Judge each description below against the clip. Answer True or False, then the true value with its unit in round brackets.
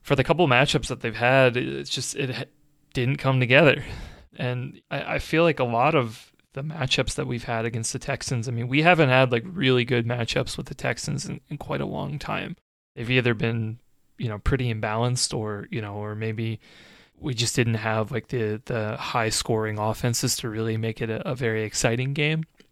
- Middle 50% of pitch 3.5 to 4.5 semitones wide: False (3.0 semitones)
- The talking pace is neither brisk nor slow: False (210 wpm)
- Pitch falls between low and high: False (125 Hz)